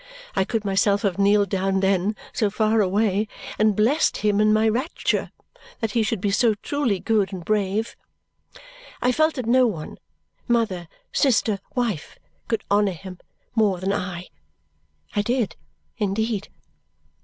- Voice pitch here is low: No, high, 210 Hz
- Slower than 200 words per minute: Yes, average, 145 wpm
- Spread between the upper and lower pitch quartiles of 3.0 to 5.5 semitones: No, narrow, 2.6 semitones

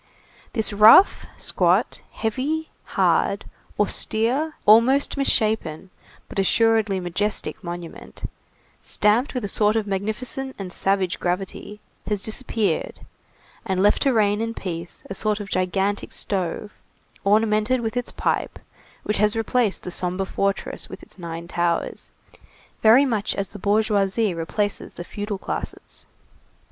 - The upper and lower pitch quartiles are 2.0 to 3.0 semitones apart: Yes, average, 2.7 semitones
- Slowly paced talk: Yes, slow, 130 wpm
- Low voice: No, high, 210 Hz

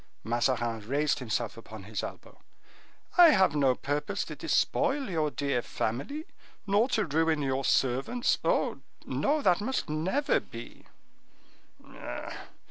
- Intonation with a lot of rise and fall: Yes, wide, 8.9 semitones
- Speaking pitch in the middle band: Yes, medium, 150 Hz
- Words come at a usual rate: No, slow, 125 wpm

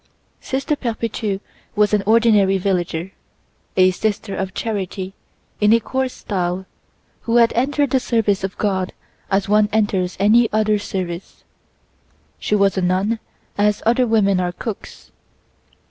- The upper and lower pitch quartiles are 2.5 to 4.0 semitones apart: Yes, average, 3.1 semitones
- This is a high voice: Yes, high, 205 Hz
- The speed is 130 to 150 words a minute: Yes, slow, 135 wpm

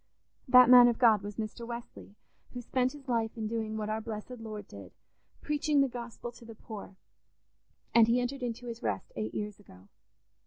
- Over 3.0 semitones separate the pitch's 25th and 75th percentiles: No, narrow, 2.5 semitones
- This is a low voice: No, high, 230 Hz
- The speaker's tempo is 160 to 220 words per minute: Yes, average, 180 wpm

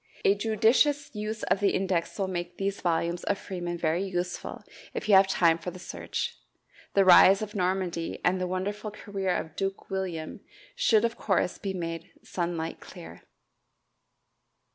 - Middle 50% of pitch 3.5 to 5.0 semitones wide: No, narrow, 2.5 semitones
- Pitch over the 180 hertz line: Yes, high, 190 Hz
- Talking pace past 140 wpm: Yes, average, 160 wpm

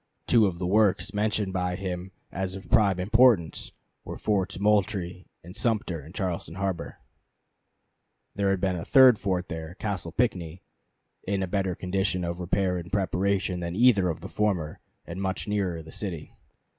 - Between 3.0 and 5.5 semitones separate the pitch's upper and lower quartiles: No, narrow, 2.4 semitones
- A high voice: No, very low, 95 Hz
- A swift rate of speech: No, average, 165 wpm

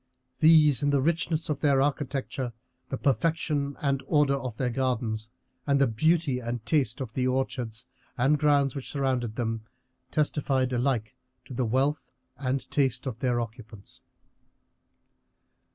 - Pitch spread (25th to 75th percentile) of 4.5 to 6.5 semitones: No, average, 3.0 semitones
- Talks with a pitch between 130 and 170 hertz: Yes, low, 135 Hz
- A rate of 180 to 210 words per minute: No, average, 140 wpm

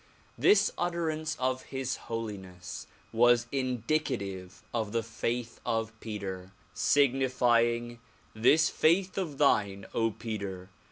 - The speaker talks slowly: Yes, slow, 105 wpm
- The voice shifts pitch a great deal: No, average, 4.3 semitones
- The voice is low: Yes, low, 120 Hz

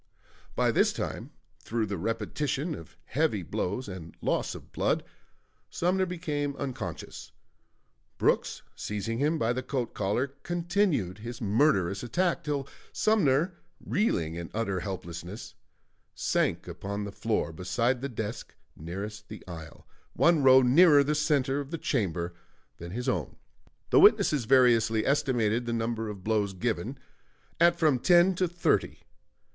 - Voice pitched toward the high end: No, low, 120 Hz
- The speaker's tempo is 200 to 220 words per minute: No, average, 140 wpm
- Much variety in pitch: Yes, wide, 6.5 semitones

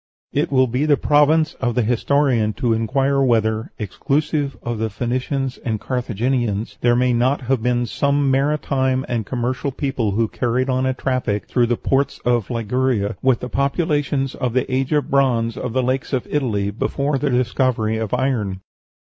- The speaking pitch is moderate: No, low, 125 Hz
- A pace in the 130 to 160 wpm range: No, average, 170 wpm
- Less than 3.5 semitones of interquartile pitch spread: Yes, average, 2.8 semitones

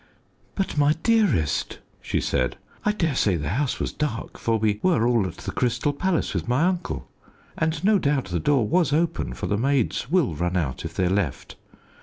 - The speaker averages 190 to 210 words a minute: Yes, average, 195 wpm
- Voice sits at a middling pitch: No, low, 130 Hz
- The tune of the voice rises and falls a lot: Yes, wide, 8.8 semitones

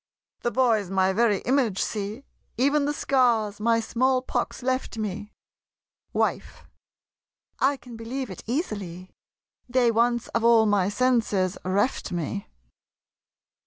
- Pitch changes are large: No, average, 3.9 semitones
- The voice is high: Yes, high, 230 Hz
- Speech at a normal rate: No, slow, 125 wpm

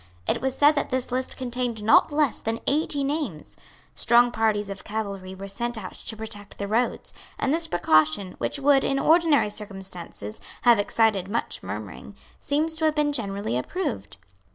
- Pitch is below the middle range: No, high, 225 Hz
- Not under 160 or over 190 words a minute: Yes, average, 170 wpm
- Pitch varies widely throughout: Yes, wide, 5.8 semitones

